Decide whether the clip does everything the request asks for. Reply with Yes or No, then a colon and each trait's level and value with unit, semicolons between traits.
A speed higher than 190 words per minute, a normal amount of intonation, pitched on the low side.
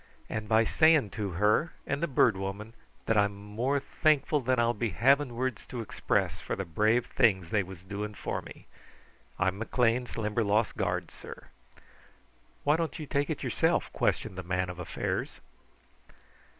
No: average, 165 wpm; average, 4.4 semitones; low, 110 Hz